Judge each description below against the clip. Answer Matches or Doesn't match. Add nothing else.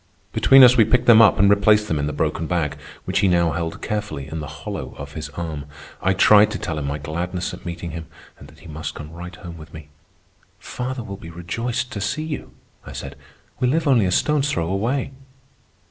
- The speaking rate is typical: Doesn't match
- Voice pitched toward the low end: Matches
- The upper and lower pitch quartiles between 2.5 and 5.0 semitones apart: Doesn't match